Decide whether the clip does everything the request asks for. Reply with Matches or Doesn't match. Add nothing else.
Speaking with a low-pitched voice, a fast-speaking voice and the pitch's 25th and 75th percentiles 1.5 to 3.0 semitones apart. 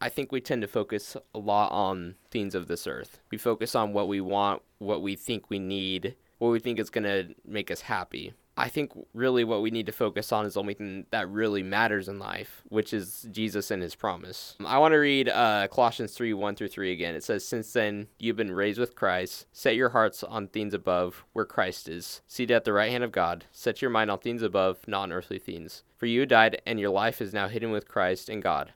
Matches